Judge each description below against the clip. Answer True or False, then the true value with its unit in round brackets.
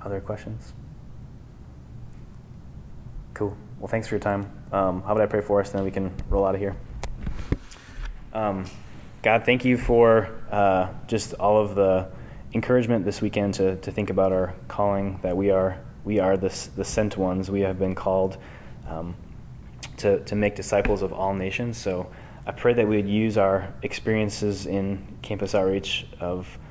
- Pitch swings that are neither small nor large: False (2.3 semitones)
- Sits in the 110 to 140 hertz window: False (100 Hz)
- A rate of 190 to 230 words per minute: False (170 wpm)